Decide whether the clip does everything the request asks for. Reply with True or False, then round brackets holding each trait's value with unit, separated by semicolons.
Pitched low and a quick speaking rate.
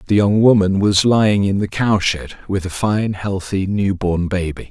False (100 Hz; 190 wpm)